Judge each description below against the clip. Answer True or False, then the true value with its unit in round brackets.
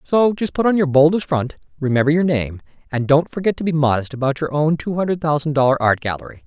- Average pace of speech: False (230 wpm)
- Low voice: False (150 Hz)